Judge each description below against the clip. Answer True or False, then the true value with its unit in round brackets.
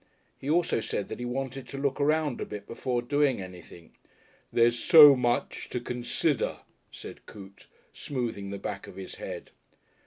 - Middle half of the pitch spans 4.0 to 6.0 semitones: True (5.1 semitones)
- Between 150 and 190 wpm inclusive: True (160 wpm)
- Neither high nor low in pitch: False (125 Hz)